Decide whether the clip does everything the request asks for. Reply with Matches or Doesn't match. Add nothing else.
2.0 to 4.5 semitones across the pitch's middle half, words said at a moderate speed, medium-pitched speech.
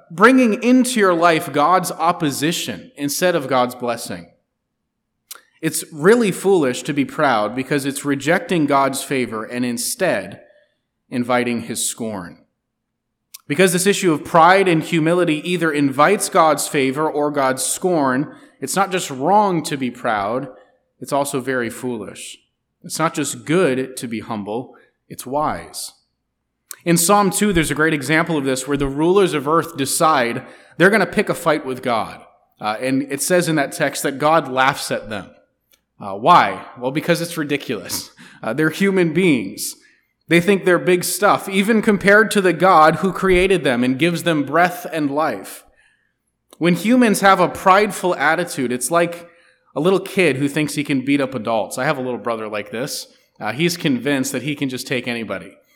Doesn't match